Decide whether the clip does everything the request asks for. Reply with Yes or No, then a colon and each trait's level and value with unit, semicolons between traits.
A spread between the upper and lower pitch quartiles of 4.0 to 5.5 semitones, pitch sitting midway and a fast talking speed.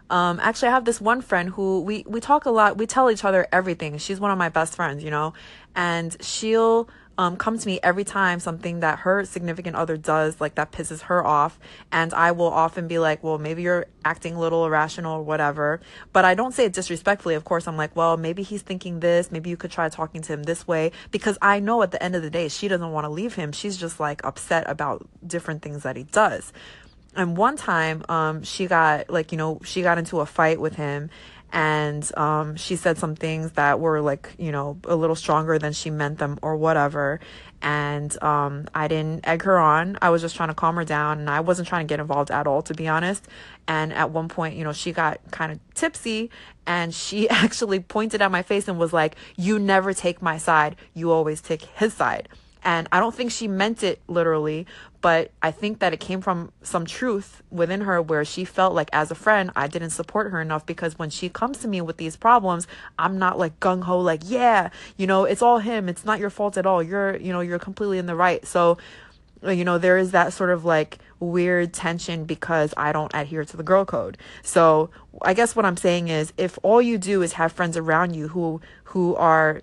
No: average, 3.0 semitones; medium, 170 Hz; fast, 235 wpm